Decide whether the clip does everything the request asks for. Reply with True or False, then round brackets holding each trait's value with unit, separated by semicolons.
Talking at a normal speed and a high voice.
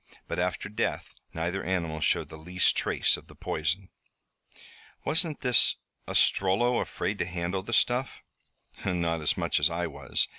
False (150 wpm; 90 Hz)